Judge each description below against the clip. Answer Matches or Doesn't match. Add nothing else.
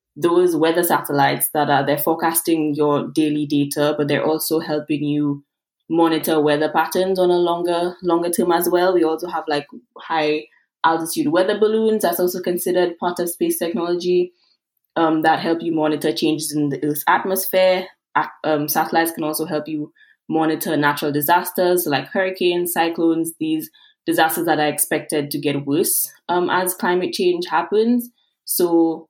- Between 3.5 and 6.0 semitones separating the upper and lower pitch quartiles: Doesn't match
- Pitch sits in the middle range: Matches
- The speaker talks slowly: Doesn't match